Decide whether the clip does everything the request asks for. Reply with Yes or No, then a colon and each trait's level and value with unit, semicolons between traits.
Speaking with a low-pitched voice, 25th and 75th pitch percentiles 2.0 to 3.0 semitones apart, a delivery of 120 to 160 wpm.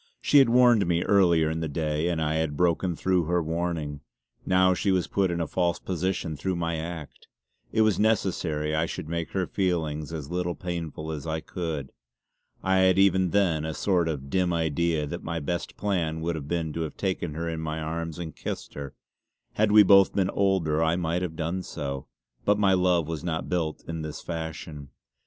No: very low, 85 Hz; narrow, 2.6 semitones; average, 200 wpm